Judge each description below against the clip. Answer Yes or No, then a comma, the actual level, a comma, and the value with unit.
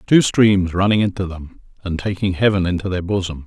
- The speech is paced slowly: No, average, 190 wpm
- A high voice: No, very low, 95 Hz